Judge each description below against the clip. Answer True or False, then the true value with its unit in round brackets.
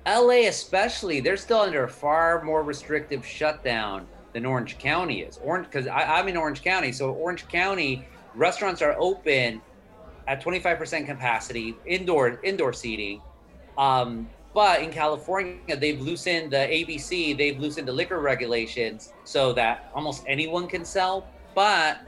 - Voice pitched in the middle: True (150 Hz)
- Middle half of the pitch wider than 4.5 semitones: True (5.3 semitones)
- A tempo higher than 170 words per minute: False (140 wpm)